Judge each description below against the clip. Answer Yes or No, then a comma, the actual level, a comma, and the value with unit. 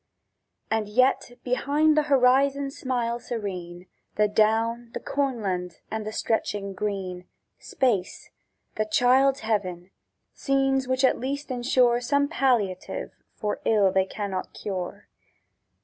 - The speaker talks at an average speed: No, slow, 115 wpm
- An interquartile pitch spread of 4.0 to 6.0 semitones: Yes, average, 4.7 semitones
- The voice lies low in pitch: No, high, 230 Hz